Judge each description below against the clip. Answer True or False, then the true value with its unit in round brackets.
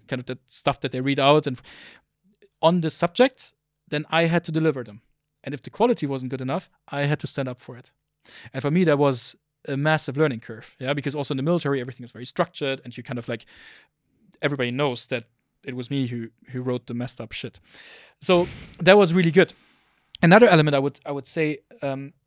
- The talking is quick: True (220 wpm)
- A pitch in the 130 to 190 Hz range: True (140 Hz)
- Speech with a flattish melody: False (3.7 semitones)